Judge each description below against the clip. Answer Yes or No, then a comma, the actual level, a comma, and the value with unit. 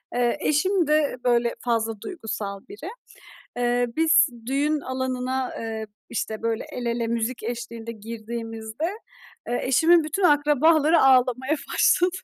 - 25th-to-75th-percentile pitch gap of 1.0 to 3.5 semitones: No, average, 4.6 semitones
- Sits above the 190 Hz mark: Yes, very high, 250 Hz